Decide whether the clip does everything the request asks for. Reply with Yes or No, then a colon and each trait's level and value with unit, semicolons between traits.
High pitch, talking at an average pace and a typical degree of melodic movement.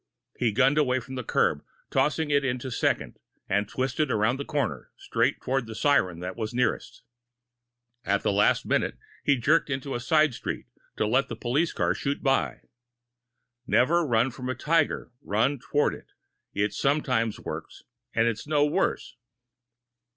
No: low, 130 Hz; average, 165 wpm; average, 4.1 semitones